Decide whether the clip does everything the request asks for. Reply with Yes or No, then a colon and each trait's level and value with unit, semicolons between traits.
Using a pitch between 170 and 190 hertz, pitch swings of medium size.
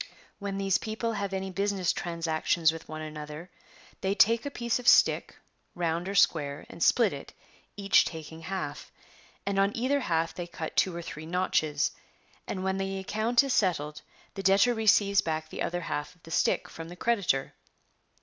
Yes: medium, 185 Hz; average, 3.8 semitones